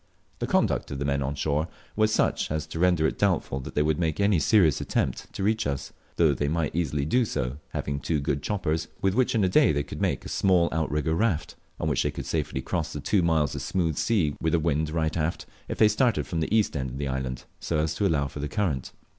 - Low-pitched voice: Yes, very low, 80 Hz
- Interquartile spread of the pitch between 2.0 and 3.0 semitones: No, average, 4.1 semitones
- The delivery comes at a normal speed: No, fast, 250 wpm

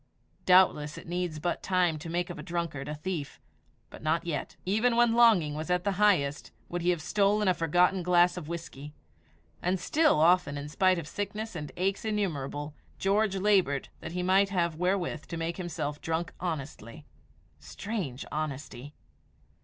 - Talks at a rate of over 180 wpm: No, average, 170 wpm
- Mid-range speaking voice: Yes, medium, 175 Hz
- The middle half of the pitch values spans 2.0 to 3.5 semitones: No, average, 3.9 semitones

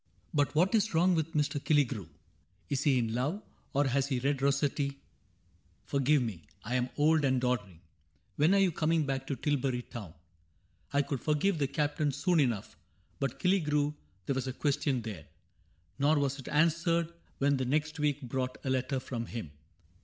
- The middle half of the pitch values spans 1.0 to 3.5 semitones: Yes, average, 3.1 semitones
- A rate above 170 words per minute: Yes, average, 185 wpm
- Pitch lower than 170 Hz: Yes, medium, 140 Hz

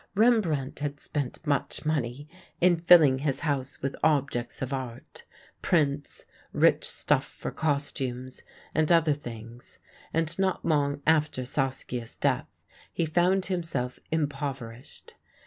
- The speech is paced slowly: Yes, slow, 120 wpm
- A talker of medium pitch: Yes, medium, 145 Hz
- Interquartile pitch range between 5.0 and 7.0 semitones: No, average, 3.5 semitones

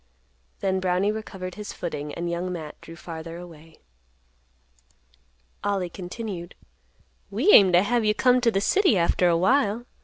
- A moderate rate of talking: Yes, average, 150 wpm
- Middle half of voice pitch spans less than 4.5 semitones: Yes, average, 3.7 semitones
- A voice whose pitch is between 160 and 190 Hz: Yes, medium, 185 Hz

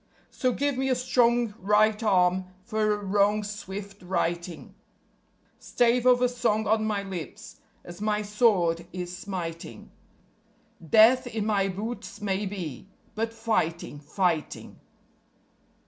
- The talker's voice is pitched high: Yes, high, 205 Hz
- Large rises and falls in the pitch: No, average, 3.8 semitones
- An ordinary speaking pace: No, slow, 125 wpm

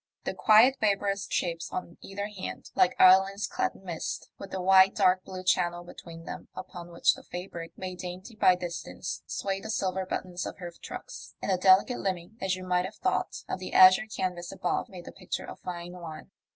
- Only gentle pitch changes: Yes, narrow, 1.6 semitones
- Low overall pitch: No, medium, 185 Hz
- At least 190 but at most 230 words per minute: Yes, average, 200 wpm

